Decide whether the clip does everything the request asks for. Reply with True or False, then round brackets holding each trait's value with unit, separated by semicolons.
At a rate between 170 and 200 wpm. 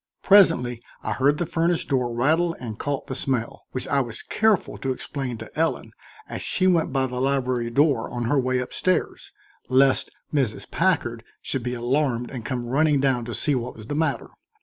True (195 wpm)